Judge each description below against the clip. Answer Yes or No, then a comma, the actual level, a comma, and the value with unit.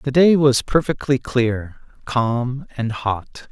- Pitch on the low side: Yes, low, 125 Hz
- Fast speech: No, slow, 135 wpm